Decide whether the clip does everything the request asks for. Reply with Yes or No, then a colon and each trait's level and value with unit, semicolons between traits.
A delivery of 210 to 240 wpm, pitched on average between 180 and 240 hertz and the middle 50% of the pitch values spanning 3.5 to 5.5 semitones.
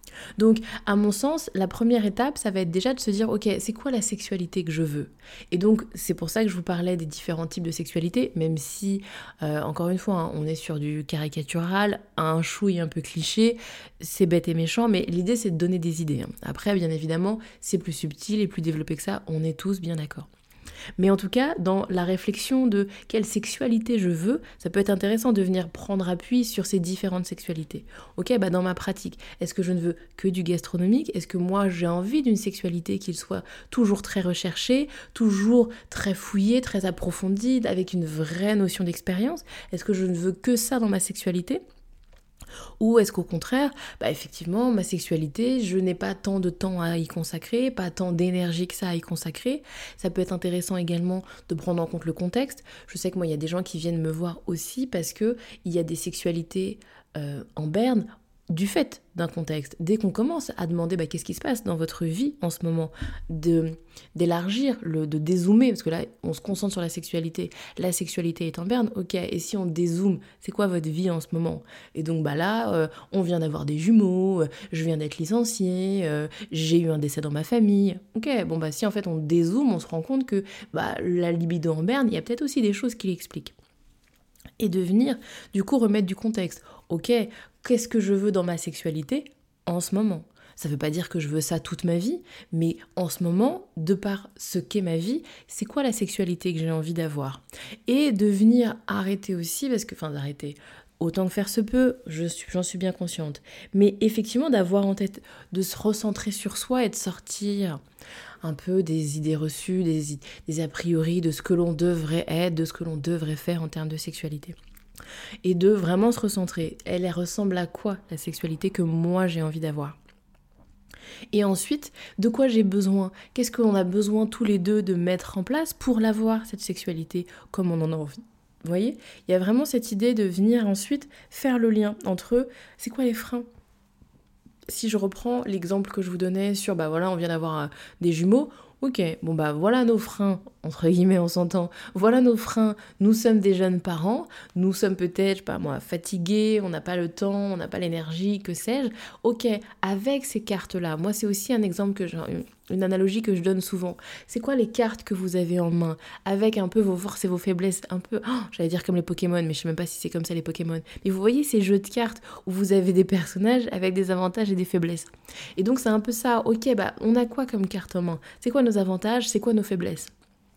Yes: fast, 220 wpm; high, 190 Hz; average, 4.2 semitones